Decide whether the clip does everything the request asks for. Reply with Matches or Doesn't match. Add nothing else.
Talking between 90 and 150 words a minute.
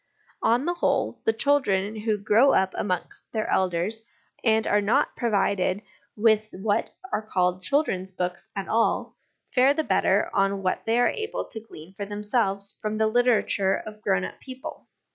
Doesn't match